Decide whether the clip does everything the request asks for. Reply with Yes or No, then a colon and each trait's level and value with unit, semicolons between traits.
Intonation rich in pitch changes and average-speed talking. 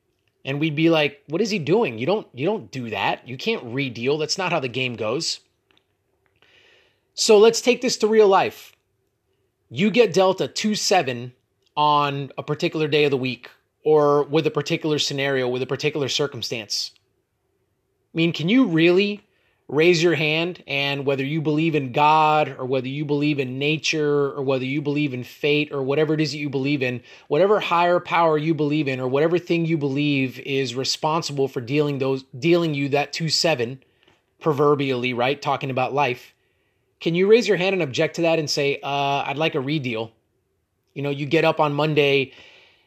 No: average, 3.2 semitones; average, 190 wpm